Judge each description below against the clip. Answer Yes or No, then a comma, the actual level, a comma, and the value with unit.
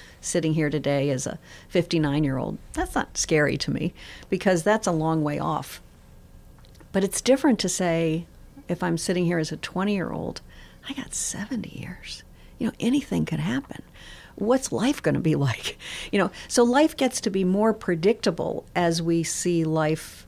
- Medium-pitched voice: Yes, medium, 180 Hz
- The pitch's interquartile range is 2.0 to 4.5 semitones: No, wide, 5.6 semitones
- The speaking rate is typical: Yes, average, 180 wpm